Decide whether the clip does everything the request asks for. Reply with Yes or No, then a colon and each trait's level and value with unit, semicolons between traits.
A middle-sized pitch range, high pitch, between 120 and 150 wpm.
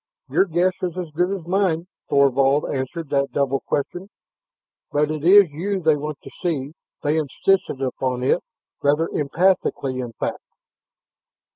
No: average, 4.3 semitones; medium, 155 Hz; average, 145 wpm